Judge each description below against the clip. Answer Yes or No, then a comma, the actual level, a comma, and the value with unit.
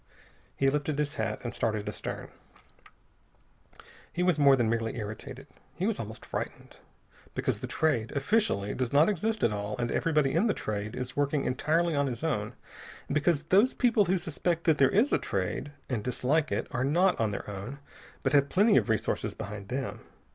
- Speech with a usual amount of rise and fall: No, wide, 6.4 semitones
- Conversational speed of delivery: Yes, average, 185 wpm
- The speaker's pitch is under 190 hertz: Yes, medium, 140 Hz